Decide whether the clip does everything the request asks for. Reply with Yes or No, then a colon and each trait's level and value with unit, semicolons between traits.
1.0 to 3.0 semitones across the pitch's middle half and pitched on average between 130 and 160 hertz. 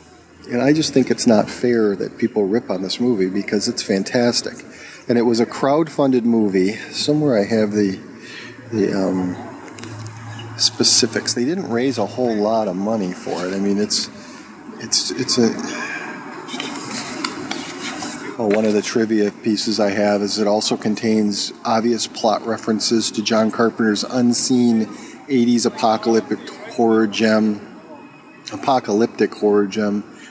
No: narrow, 2.5 semitones; low, 110 Hz